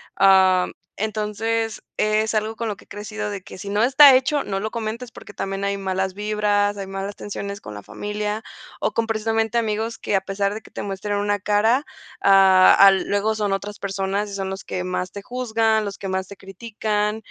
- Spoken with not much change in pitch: Yes, narrow, 2.0 semitones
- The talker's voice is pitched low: No, high, 205 Hz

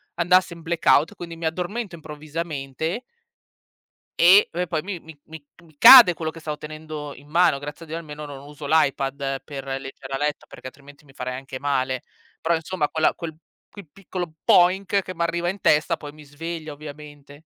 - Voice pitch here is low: No, medium, 155 Hz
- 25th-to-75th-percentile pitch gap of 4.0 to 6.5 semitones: No, average, 2.9 semitones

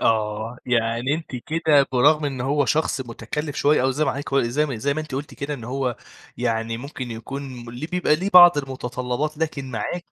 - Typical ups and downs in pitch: Yes, average, 3.8 semitones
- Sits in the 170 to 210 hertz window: No, low, 135 Hz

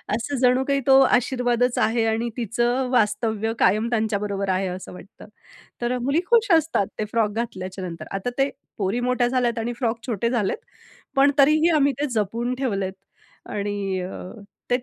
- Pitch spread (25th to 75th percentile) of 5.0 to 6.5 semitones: No, average, 3.7 semitones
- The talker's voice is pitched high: Yes, high, 235 Hz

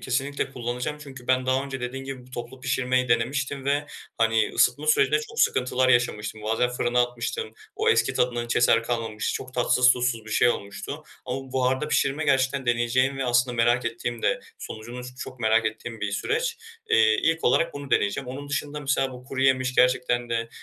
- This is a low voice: Yes, low, 125 Hz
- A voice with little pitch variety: Yes, narrow, 2.1 semitones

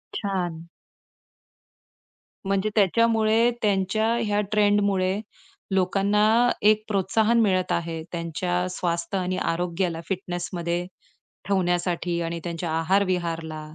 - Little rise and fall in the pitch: No, average, 3.2 semitones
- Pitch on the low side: No, medium, 185 Hz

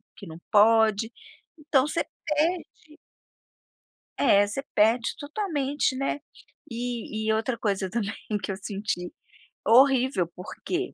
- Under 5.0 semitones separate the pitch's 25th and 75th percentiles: No, wide, 5.5 semitones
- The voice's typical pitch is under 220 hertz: No, high, 230 Hz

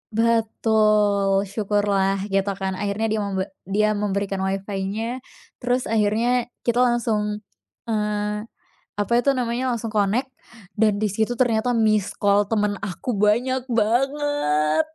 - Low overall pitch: No, high, 215 Hz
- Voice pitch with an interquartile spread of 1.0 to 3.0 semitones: Yes, average, 2.7 semitones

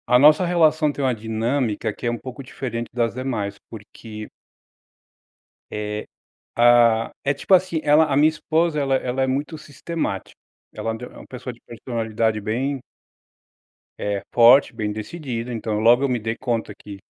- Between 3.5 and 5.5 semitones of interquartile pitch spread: Yes, average, 4.0 semitones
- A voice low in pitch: Yes, low, 120 Hz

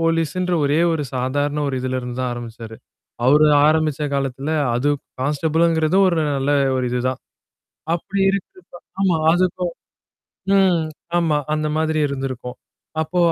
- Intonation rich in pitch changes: No, average, 4.1 semitones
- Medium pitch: Yes, medium, 150 Hz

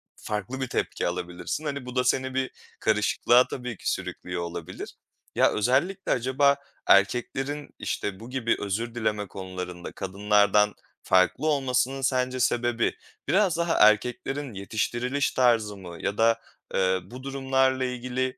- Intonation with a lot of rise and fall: No, average, 4.3 semitones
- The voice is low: Yes, low, 120 Hz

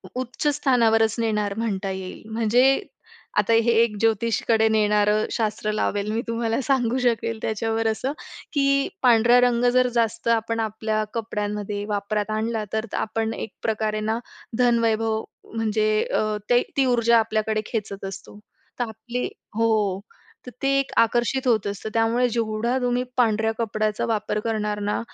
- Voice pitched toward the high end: Yes, high, 225 Hz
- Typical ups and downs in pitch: No, narrow, 1.6 semitones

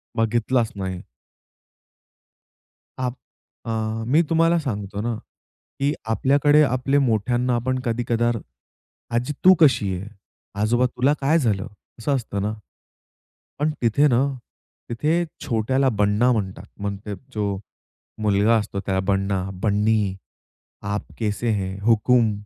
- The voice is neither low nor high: No, low, 115 Hz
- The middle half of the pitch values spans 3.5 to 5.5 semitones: Yes, average, 4.0 semitones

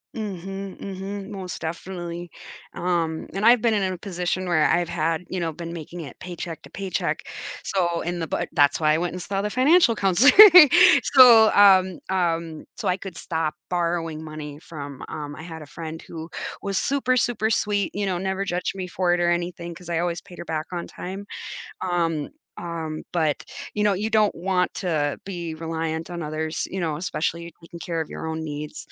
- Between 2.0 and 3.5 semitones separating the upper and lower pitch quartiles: Yes, average, 3.0 semitones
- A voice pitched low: No, medium, 175 Hz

